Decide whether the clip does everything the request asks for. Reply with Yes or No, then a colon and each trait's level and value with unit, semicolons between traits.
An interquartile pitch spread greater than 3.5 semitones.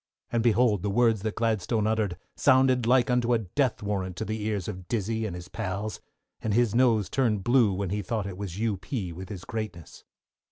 No: average, 3.1 semitones